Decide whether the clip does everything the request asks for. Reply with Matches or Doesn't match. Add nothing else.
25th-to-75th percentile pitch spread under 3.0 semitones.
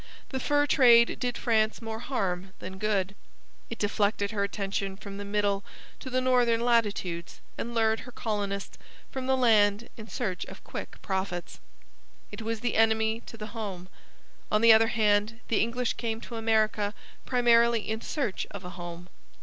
Matches